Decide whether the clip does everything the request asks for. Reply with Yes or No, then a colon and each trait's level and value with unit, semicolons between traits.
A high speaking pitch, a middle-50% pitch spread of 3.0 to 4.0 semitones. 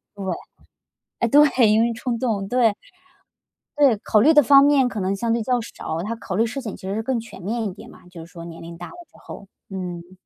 No: high, 220 Hz; average, 4.6 semitones